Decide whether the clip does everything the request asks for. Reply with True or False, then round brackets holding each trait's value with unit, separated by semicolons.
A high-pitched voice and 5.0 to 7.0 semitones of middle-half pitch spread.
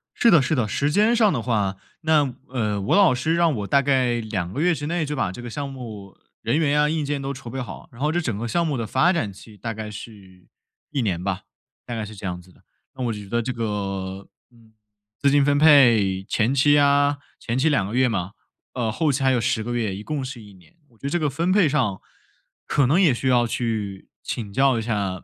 False (125 Hz; 5.4 semitones)